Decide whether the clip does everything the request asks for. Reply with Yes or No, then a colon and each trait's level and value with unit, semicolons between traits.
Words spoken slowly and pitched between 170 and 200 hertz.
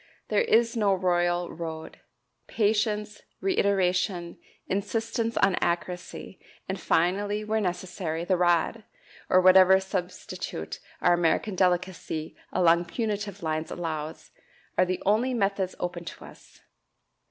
Yes: slow, 115 wpm; medium, 185 Hz